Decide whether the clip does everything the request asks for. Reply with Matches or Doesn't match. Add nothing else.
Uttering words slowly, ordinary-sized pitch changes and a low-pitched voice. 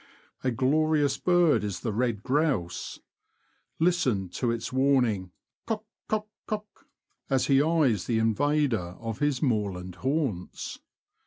Doesn't match